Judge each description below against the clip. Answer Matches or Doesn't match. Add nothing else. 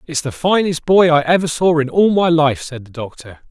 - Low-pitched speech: Doesn't match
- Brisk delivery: Matches